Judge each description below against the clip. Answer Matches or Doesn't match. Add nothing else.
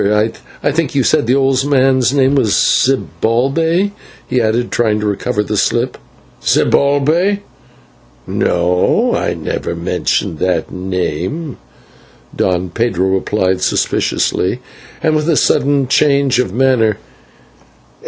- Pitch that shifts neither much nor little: Doesn't match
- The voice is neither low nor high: Doesn't match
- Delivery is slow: Matches